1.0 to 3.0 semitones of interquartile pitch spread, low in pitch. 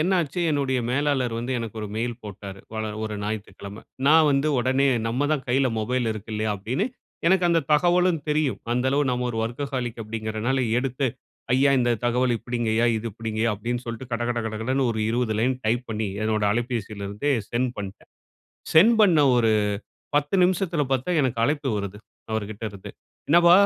No: average, 4.4 semitones; low, 120 Hz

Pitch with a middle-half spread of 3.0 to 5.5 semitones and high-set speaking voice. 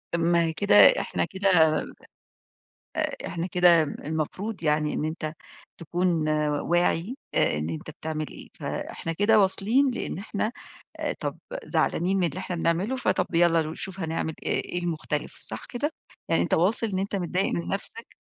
No: average, 3.5 semitones; medium, 175 Hz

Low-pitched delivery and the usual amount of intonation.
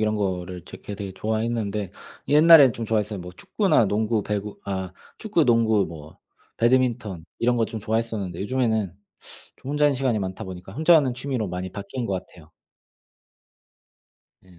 Yes: low, 110 Hz; average, 4.2 semitones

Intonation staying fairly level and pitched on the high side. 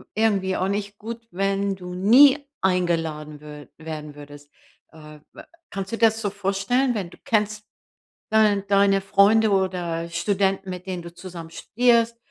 No: average, 3.7 semitones; high, 195 Hz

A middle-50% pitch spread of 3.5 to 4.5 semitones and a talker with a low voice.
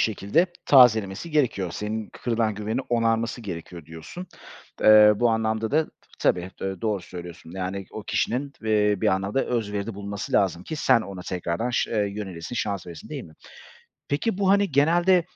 Yes: average, 4.2 semitones; low, 110 Hz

